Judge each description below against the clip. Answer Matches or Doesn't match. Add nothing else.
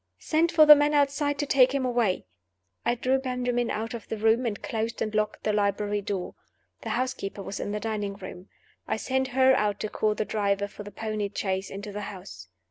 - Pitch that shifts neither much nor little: Matches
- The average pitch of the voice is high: Matches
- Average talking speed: Doesn't match